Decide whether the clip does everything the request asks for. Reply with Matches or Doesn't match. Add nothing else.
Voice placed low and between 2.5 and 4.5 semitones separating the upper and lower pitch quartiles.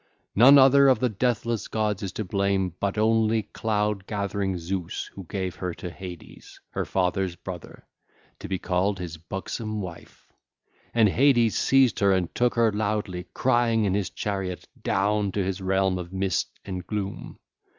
Matches